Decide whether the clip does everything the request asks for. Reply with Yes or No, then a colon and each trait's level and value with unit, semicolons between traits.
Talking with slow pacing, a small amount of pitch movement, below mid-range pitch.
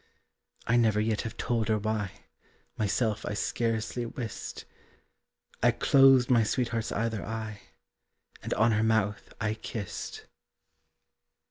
Yes: slow, 120 wpm; narrow, 1.5 semitones; low, 110 Hz